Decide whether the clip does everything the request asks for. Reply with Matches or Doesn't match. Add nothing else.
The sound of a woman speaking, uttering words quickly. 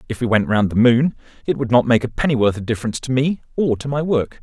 Doesn't match